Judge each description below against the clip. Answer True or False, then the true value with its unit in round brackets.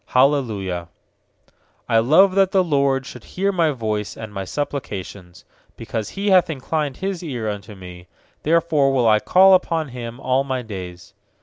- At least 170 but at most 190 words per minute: True (180 wpm)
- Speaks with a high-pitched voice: False (130 Hz)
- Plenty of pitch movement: True (7.2 semitones)